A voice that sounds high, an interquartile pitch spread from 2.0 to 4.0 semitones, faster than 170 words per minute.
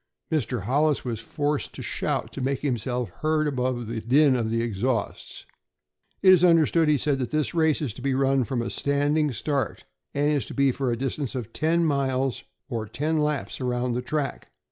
No: low, 135 Hz; average, 3.4 semitones; average, 195 wpm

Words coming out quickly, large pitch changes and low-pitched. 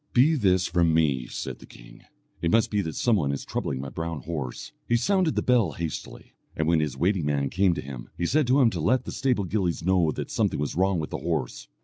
Yes: fast, 245 wpm; wide, 6.1 semitones; very low, 85 Hz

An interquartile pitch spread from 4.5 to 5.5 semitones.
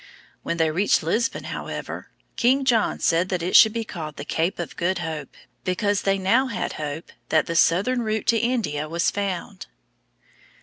Yes: average, 5.2 semitones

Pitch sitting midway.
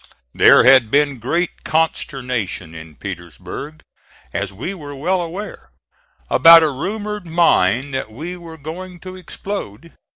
Yes: medium, 155 Hz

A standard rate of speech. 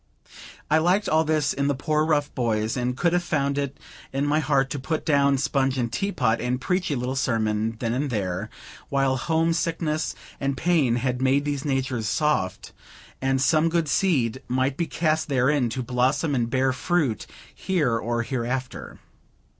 Yes: average, 175 wpm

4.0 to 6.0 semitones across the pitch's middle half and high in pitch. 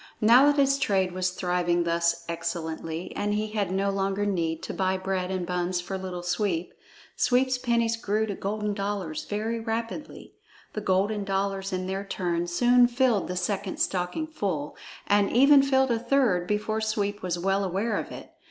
No: average, 3.4 semitones; high, 195 Hz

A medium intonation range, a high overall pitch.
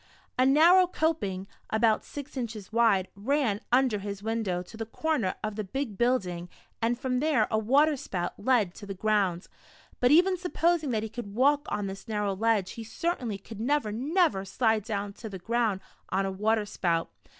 Yes: average, 4.8 semitones; high, 220 Hz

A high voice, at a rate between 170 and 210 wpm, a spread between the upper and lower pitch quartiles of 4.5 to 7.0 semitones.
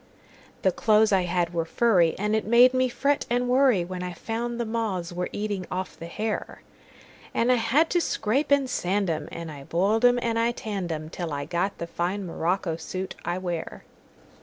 Yes: high, 195 Hz; average, 180 wpm; average, 5.1 semitones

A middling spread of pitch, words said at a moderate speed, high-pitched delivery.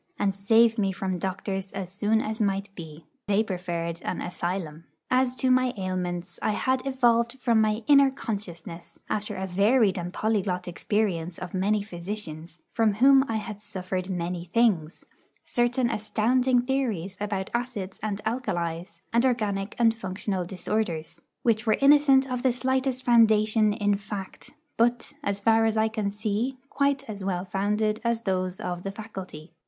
Yes: average, 4.0 semitones; average, 160 wpm; high, 210 Hz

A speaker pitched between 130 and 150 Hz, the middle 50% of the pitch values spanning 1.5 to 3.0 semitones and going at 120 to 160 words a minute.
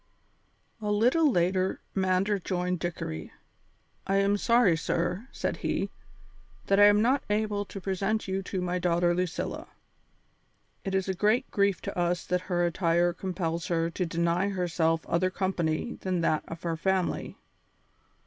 No: medium, 185 Hz; narrow, 2.6 semitones; average, 150 wpm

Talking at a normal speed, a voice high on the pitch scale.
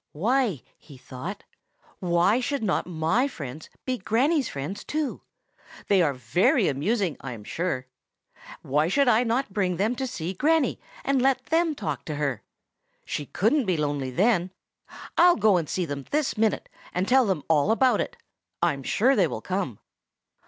Yes: average, 165 wpm; high, 195 Hz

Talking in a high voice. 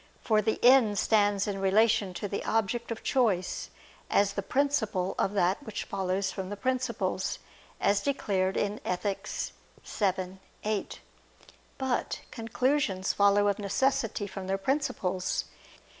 Yes: high, 205 Hz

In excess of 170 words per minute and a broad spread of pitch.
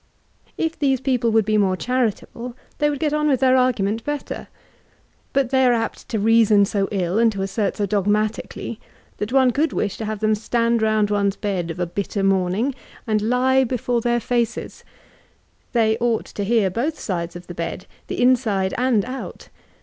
No: average, 190 wpm; average, 3.8 semitones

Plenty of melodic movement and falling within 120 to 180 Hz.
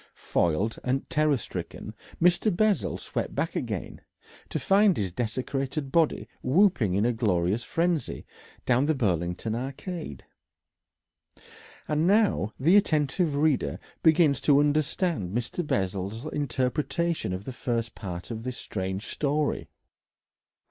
Yes: wide, 6.6 semitones; low, 135 Hz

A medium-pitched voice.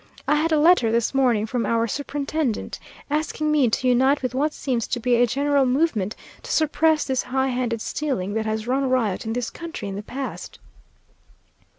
No: very high, 255 Hz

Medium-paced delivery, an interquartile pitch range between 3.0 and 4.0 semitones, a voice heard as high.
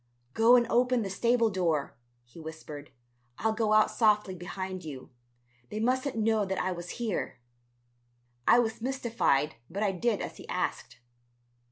No: average, 155 wpm; average, 4.8 semitones; high, 210 Hz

